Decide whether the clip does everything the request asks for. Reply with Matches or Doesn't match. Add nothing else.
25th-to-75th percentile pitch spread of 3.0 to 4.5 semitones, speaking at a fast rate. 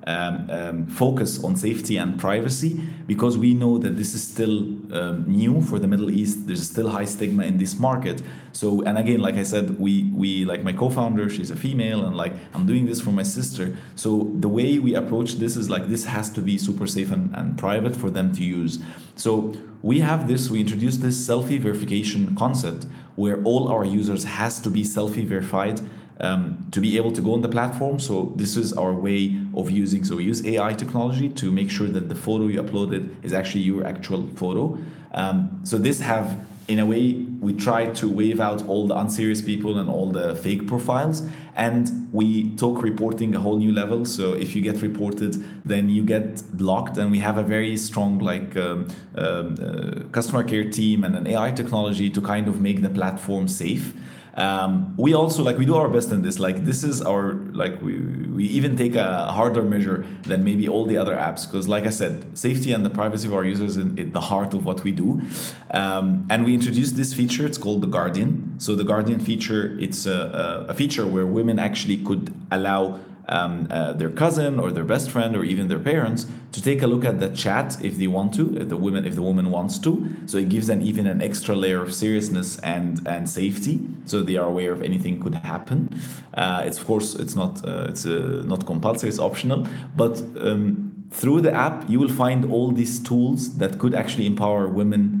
Matches